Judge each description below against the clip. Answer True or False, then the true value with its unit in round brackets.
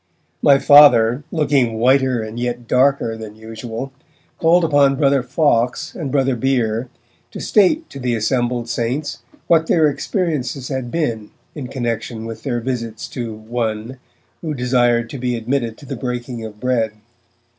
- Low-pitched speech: True (125 Hz)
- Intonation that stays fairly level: False (3.2 semitones)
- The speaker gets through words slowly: False (150 wpm)